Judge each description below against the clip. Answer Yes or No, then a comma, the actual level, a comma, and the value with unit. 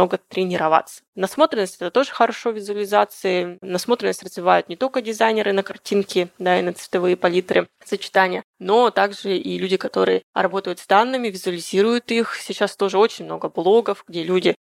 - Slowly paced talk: No, average, 150 wpm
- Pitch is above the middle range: Yes, high, 195 Hz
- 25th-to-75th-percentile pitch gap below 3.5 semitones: Yes, average, 3.0 semitones